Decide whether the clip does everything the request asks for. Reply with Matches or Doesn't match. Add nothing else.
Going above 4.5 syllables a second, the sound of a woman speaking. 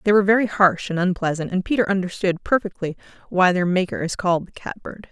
Matches